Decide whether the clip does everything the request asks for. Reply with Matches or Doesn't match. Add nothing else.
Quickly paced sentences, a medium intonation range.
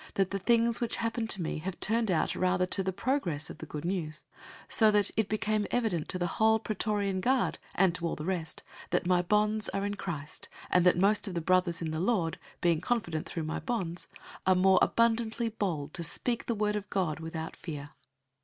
Matches